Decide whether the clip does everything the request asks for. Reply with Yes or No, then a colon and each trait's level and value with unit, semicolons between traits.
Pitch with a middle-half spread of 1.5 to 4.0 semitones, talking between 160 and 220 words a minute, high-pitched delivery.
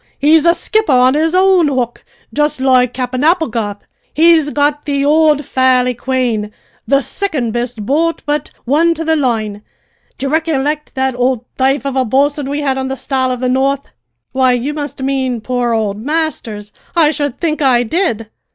Yes: average, 3.2 semitones; average, 175 wpm; very high, 270 Hz